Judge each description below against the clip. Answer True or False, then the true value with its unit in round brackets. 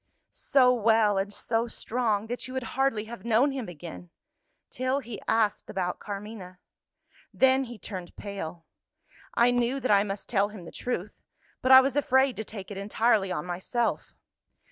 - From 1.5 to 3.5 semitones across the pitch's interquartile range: False (4.0 semitones)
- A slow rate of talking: False (165 wpm)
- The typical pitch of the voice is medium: False (220 Hz)